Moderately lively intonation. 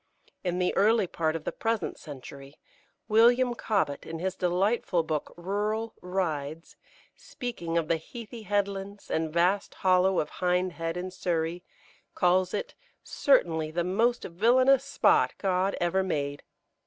Yes: average, 4.3 semitones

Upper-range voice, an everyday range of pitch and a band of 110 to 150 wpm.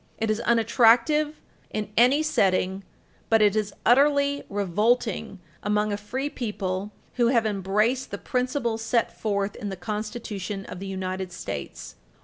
Yes: high, 215 Hz; average, 3.4 semitones; average, 140 wpm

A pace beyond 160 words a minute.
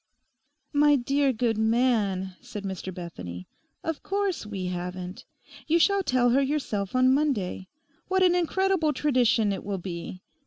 No: average, 145 wpm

